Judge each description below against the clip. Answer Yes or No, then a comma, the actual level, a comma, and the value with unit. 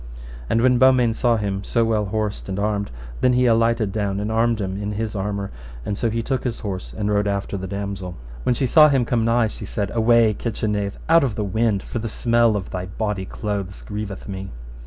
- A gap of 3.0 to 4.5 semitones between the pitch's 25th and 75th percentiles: No, narrow, 2.6 semitones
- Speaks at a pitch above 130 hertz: No, low, 105 Hz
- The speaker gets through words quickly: Yes, fast, 220 wpm